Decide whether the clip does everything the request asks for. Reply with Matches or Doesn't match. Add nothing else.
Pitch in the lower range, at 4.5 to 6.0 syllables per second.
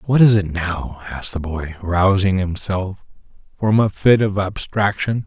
Doesn't match